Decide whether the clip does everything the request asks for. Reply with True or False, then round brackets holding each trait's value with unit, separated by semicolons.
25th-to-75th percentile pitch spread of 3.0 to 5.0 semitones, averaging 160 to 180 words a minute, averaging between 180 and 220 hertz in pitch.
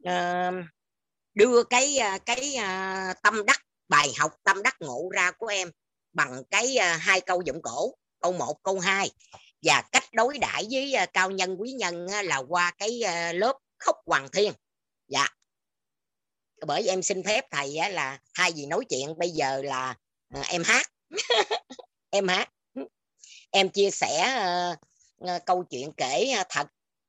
True (4.0 semitones; 170 wpm; 185 Hz)